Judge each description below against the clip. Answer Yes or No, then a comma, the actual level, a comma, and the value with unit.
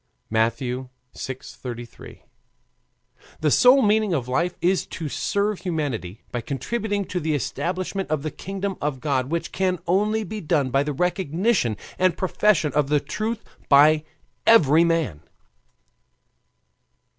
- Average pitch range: No, wide, 5.9 semitones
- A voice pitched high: No, medium, 160 Hz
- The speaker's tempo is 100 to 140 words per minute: Yes, slow, 135 wpm